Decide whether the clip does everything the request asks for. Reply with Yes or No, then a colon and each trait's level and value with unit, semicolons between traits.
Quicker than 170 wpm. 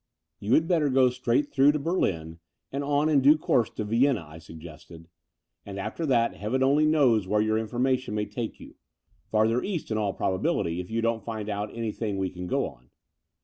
Yes: average, 200 wpm